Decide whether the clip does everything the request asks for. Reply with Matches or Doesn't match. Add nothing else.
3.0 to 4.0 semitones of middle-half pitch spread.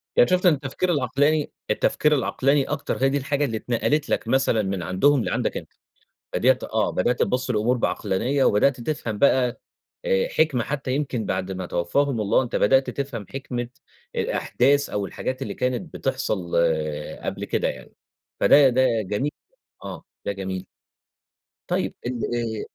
Doesn't match